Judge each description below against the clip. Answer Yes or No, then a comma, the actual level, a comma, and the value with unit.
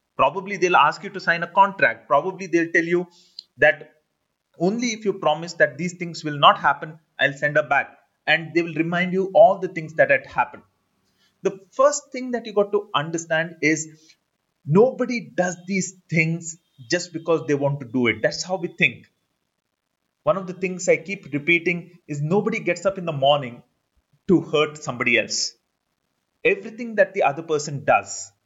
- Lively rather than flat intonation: No, average, 3.9 semitones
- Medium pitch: Yes, medium, 170 Hz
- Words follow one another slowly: No, average, 180 wpm